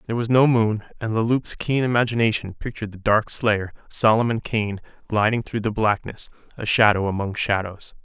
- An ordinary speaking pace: Yes, average, 170 wpm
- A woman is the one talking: No, male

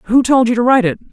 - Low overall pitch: No, high, 240 Hz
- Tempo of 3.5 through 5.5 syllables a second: No, 7.2 syllables/s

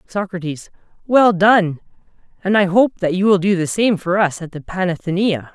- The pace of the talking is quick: No, average, 185 wpm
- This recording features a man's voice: Yes, male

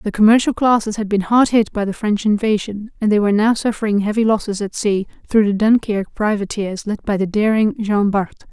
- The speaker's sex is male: No, female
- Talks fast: Yes, fast, 210 wpm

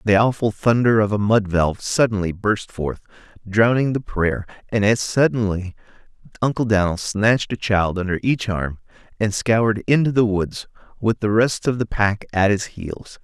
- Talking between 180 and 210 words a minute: No, average, 170 wpm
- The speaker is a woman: No, male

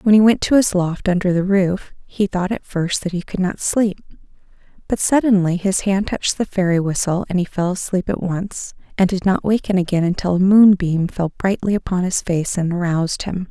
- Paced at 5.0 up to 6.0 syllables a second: Yes, 5.1 syllables/s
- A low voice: No, medium, 185 Hz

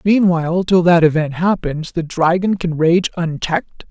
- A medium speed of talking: Yes, average, 155 wpm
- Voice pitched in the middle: Yes, medium, 170 Hz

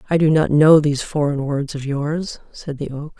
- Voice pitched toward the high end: No, medium, 150 Hz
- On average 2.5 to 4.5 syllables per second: No, 5.0 syllables/s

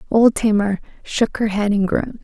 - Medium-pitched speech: No, high, 210 Hz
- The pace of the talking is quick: No, average, 190 wpm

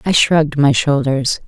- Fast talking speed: No, average, 165 wpm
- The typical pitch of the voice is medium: Yes, medium, 145 Hz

